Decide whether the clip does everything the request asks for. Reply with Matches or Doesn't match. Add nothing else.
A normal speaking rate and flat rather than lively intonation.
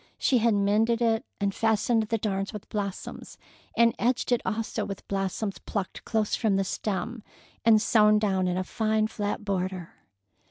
Matches